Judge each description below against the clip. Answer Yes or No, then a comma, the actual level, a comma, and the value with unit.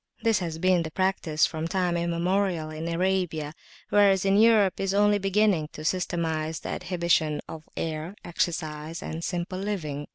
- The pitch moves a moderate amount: Yes, average, 3.3 semitones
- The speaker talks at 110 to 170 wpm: Yes, average, 150 wpm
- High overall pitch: No, medium, 175 Hz